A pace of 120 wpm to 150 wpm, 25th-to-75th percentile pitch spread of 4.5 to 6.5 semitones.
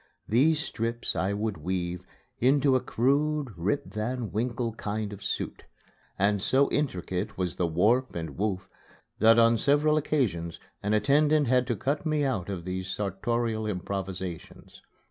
Yes: average, 145 wpm; wide, 5.6 semitones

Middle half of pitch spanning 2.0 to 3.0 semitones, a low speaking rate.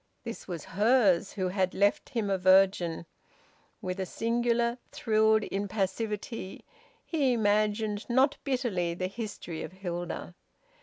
No: average, 3.7 semitones; slow, 120 wpm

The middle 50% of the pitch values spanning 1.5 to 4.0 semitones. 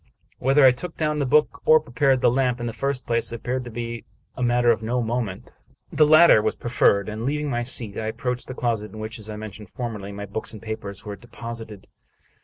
Yes: average, 2.9 semitones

